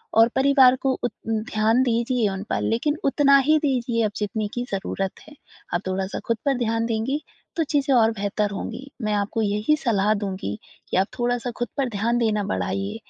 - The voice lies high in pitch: Yes, high, 225 Hz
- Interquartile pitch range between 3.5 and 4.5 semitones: Yes, average, 3.8 semitones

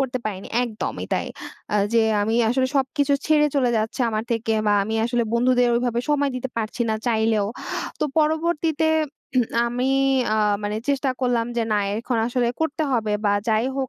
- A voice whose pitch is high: Yes, high, 245 Hz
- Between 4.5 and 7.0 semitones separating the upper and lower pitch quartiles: No, average, 3.4 semitones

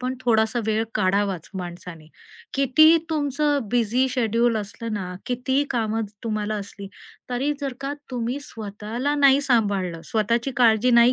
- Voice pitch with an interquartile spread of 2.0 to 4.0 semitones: Yes, average, 3.7 semitones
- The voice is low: No, high, 230 Hz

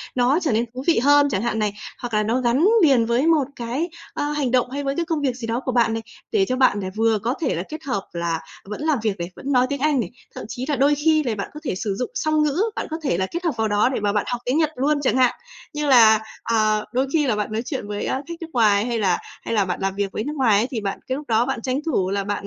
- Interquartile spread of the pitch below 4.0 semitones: No, average, 5.0 semitones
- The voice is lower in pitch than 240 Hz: No, high, 245 Hz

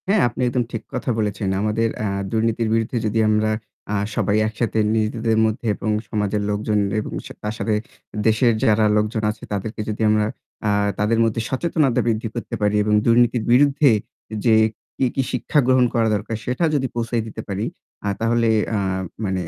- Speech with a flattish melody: Yes, narrow, 1.9 semitones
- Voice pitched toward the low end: Yes, low, 110 Hz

